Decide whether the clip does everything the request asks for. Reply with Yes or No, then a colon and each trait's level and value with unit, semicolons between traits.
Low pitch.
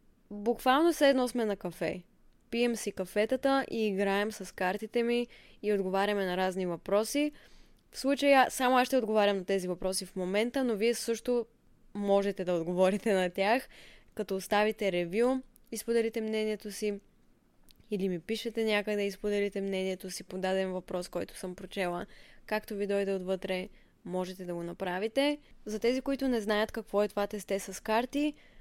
No: high, 210 Hz